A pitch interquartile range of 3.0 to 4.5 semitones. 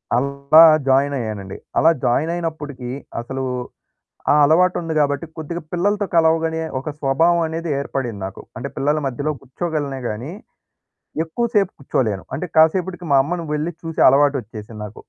Yes: average, 3.7 semitones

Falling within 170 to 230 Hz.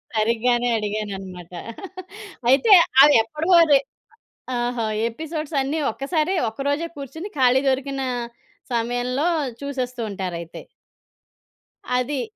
No: very high, 255 Hz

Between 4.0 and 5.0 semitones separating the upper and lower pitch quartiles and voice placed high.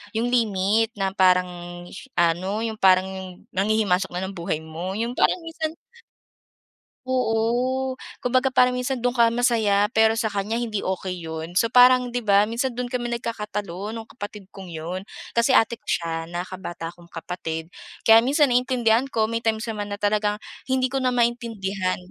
Yes: average, 4.5 semitones; high, 220 Hz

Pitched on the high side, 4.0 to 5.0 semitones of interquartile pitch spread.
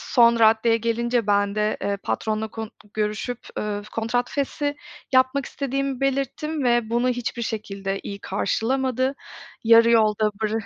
No: high, 230 Hz; average, 3.2 semitones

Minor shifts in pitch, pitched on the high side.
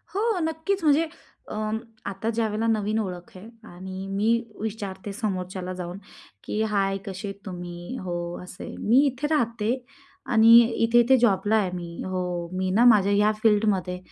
No: average, 3.3 semitones; high, 205 Hz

